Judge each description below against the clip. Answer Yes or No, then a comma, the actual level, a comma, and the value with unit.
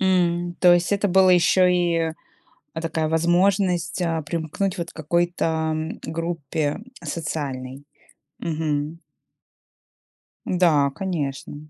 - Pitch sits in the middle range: Yes, medium, 170 Hz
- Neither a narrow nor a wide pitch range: No, narrow, 2.1 semitones